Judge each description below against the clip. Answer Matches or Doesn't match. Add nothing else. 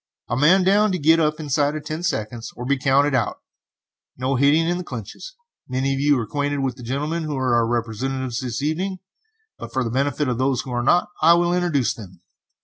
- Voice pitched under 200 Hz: Matches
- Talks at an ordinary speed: Doesn't match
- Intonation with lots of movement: Doesn't match